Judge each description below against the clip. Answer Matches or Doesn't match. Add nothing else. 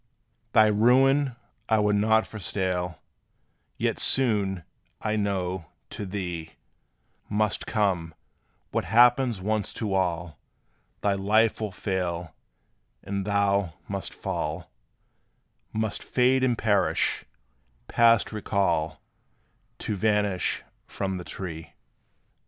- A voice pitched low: Matches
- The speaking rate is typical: Doesn't match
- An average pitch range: Matches